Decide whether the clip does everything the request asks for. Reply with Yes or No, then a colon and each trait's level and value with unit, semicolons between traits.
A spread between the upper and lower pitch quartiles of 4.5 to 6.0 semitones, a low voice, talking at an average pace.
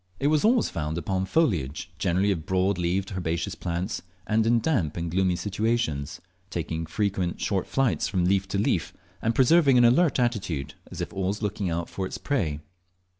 Yes: average, 5.1 semitones; very low, 95 Hz; average, 175 wpm